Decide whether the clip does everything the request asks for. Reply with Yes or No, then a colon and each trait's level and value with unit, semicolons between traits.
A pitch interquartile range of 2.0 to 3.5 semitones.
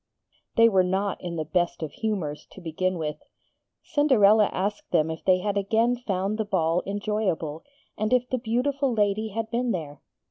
No: average, 4.2 semitones